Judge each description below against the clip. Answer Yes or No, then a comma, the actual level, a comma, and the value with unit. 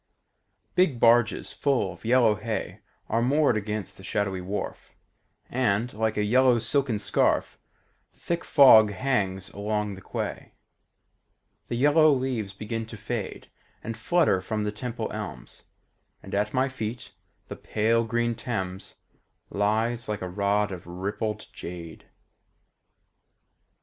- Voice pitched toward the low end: Yes, low, 110 Hz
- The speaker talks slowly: Yes, slow, 130 wpm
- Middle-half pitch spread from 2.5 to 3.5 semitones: Yes, average, 3.0 semitones